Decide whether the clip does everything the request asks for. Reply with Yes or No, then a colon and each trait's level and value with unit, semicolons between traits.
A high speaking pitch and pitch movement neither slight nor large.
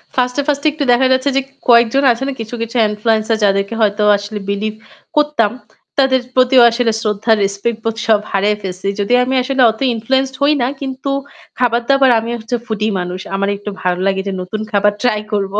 Yes: high, 225 Hz; average, 3.9 semitones